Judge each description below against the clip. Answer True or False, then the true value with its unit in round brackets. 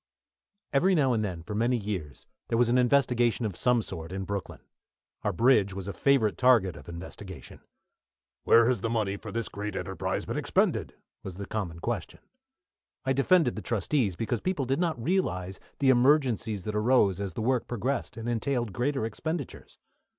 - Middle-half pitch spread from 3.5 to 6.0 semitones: True (4.7 semitones)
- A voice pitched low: True (115 Hz)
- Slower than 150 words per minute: False (175 wpm)